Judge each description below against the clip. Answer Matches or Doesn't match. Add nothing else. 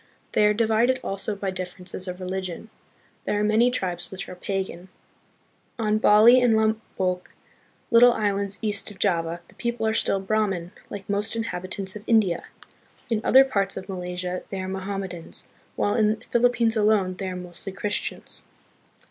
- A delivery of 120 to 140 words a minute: Doesn't match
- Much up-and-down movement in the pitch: Doesn't match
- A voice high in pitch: Matches